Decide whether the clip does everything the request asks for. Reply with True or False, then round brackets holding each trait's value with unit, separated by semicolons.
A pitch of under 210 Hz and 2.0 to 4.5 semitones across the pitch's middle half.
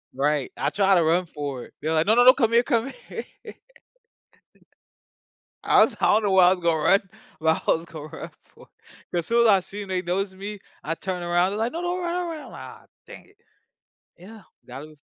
False (190 Hz; 5.5 semitones)